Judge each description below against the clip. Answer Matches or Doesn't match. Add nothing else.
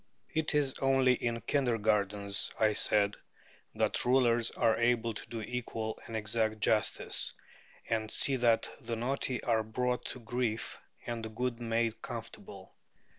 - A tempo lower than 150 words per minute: Matches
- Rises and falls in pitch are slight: Matches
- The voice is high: Doesn't match